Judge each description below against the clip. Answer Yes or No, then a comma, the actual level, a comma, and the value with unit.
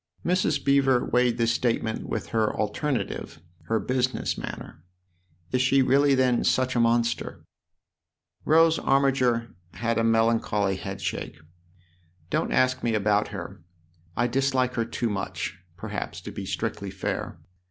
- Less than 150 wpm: Yes, average, 140 wpm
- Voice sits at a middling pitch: No, low, 115 Hz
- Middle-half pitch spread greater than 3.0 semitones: Yes, average, 3.7 semitones